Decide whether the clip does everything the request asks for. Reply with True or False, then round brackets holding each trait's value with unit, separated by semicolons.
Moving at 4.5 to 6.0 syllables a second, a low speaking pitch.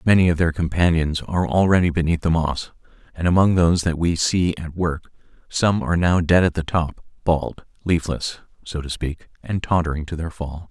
True (5.4 syllables/s; 85 Hz)